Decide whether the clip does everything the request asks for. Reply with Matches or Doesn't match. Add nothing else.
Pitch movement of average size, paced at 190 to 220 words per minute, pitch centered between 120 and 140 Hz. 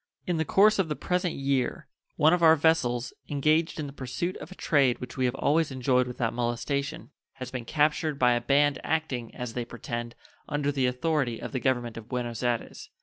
Matches